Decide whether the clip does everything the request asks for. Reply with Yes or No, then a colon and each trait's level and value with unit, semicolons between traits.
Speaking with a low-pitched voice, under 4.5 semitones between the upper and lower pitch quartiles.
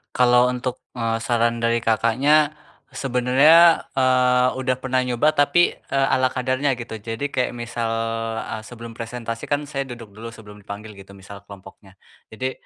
Yes: low, 120 Hz; narrow, 2.5 semitones